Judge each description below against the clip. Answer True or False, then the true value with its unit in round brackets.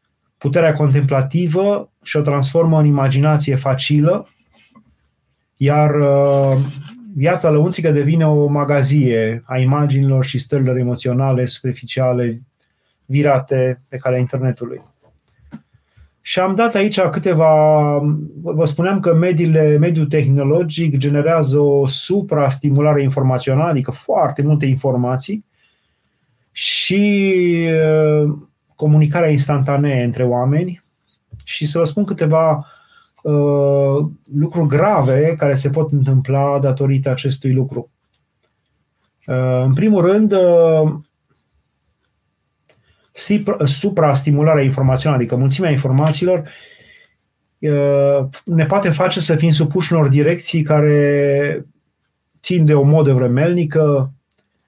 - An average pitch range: True (3.0 semitones)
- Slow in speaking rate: True (95 wpm)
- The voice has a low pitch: False (145 Hz)